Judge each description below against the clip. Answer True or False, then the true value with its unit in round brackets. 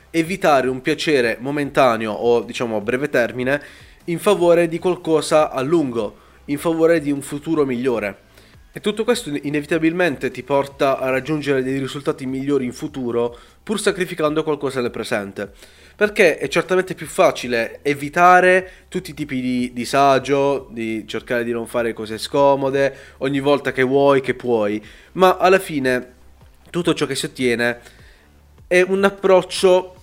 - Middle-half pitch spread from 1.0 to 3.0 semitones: False (5.2 semitones)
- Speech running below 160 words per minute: True (150 wpm)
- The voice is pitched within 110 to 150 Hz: True (140 Hz)